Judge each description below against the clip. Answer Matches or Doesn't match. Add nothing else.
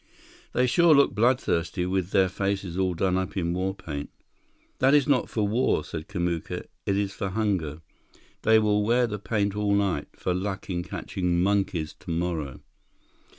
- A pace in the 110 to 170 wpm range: Matches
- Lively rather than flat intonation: Doesn't match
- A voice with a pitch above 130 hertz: Doesn't match